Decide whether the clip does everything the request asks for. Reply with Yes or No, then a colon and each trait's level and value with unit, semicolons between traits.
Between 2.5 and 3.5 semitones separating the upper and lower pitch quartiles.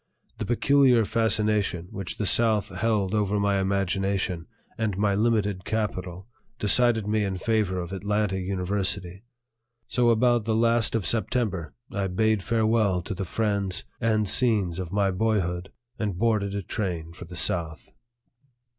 Yes: average, 2.9 semitones